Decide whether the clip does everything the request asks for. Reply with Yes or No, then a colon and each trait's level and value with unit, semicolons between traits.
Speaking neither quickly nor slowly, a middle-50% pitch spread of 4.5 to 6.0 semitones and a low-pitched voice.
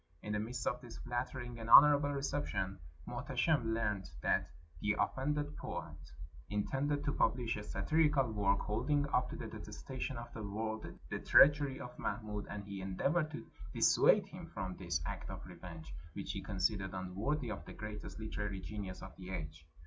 Yes: average, 170 wpm; wide, 5.4 semitones; low, 110 Hz